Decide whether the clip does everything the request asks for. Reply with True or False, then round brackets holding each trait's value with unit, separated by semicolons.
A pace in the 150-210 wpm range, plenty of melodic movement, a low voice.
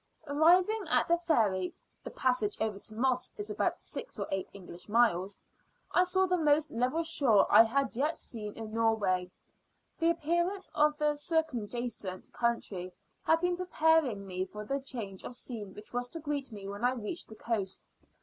False (175 wpm; 7.3 semitones; 245 Hz)